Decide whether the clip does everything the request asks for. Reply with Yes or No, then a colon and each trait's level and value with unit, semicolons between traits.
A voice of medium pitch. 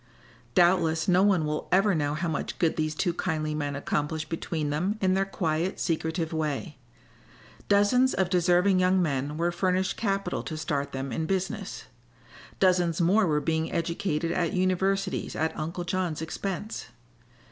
Yes: medium, 170 Hz